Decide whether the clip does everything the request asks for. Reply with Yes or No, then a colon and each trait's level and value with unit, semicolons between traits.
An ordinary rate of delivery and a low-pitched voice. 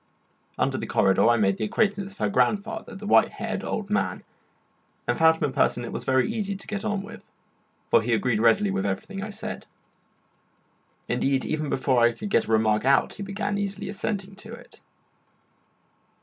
No: average, 190 wpm; high, 195 Hz